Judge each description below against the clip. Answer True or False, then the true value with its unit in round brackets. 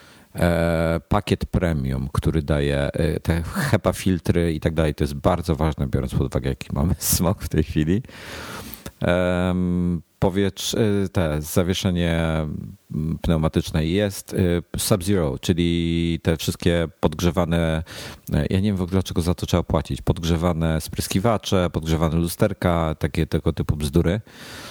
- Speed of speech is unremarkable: True (135 wpm)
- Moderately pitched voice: False (85 Hz)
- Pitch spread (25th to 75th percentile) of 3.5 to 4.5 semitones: False (2.7 semitones)